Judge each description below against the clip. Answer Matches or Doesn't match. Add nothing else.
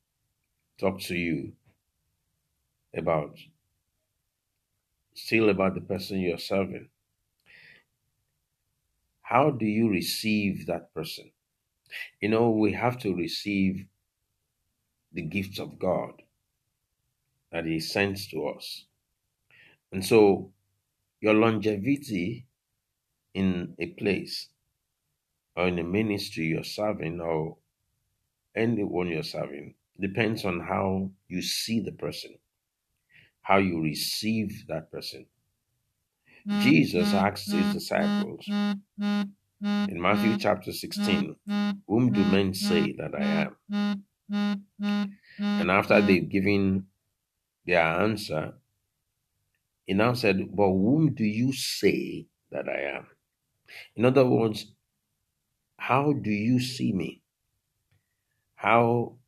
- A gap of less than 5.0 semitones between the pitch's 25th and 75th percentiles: Doesn't match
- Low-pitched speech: Matches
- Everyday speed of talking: Doesn't match